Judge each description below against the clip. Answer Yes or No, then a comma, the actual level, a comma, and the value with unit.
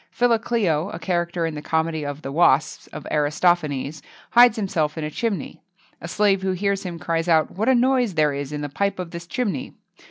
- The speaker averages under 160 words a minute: No, average, 200 wpm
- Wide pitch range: No, average, 4.7 semitones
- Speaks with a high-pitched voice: No, medium, 170 Hz